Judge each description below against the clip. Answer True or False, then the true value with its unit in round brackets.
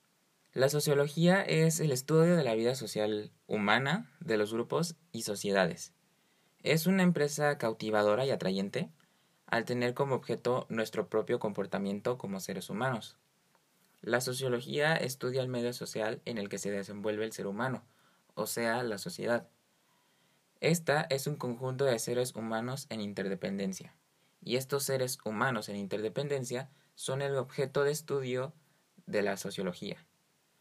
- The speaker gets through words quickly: False (140 wpm)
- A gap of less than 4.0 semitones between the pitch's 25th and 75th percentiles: False (4.7 semitones)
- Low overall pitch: True (125 Hz)